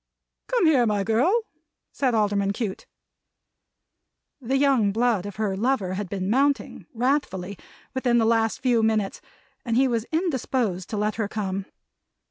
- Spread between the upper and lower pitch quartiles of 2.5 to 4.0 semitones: No, average, 4.5 semitones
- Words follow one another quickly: No, average, 145 wpm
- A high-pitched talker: Yes, high, 225 Hz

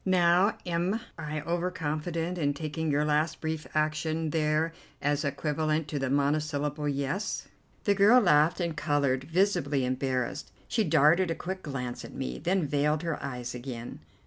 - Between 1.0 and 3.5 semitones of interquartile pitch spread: Yes, average, 2.8 semitones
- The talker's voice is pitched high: No, medium, 155 Hz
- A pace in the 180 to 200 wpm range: No, average, 155 wpm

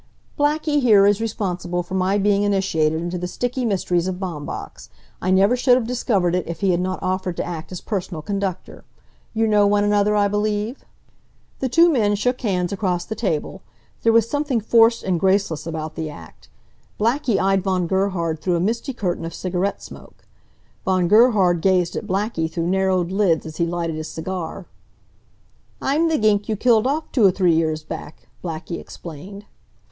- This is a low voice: No, high, 190 Hz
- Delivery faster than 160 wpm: Yes, average, 180 wpm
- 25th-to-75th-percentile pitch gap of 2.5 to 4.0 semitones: Yes, average, 3.6 semitones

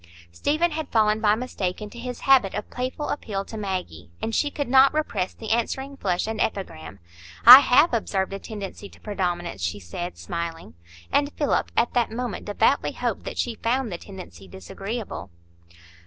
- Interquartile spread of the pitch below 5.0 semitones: No, average, 5.3 semitones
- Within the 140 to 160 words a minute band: No, average, 170 wpm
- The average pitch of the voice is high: Yes, high, 215 Hz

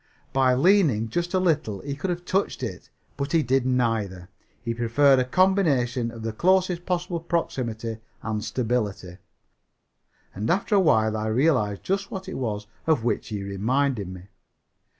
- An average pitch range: No, wide, 7.7 semitones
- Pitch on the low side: Yes, low, 125 Hz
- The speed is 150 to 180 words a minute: Yes, average, 160 wpm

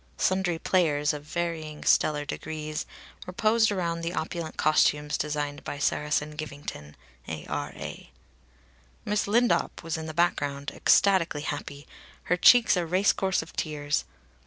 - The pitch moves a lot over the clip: No, average, 3.3 semitones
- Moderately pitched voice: Yes, medium, 155 Hz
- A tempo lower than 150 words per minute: Yes, slow, 135 wpm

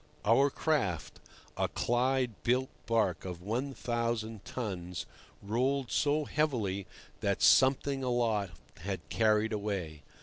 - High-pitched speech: No, low, 115 Hz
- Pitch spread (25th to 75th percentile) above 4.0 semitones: Yes, average, 4.7 semitones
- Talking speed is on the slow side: Yes, slow, 105 wpm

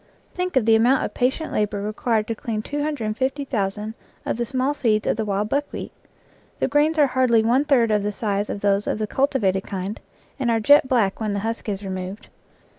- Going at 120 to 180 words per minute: No, average, 200 wpm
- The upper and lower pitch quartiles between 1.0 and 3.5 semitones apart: No, average, 4.2 semitones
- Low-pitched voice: No, high, 225 Hz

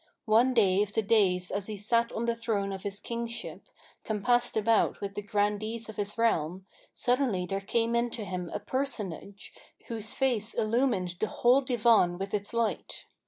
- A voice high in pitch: Yes, high, 215 Hz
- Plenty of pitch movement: No, average, 2.8 semitones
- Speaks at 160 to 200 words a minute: Yes, average, 175 wpm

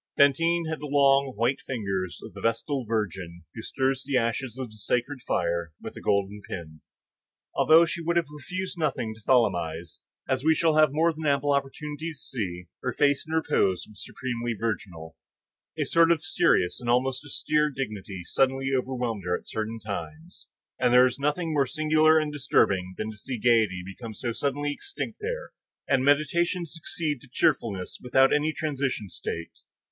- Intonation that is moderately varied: No, wide, 5.8 semitones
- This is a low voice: Yes, low, 130 Hz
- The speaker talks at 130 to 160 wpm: No, average, 175 wpm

